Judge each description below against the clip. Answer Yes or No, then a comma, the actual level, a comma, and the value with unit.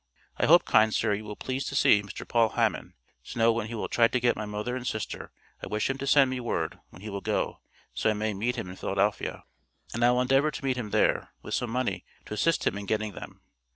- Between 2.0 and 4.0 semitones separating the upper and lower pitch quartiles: Yes, average, 3.1 semitones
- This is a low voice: Yes, low, 115 Hz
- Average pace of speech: No, fast, 255 wpm